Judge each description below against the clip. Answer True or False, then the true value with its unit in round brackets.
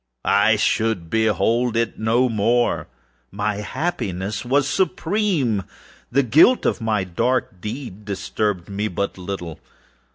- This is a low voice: True (110 Hz)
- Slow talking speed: True (120 wpm)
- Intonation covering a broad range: False (4.0 semitones)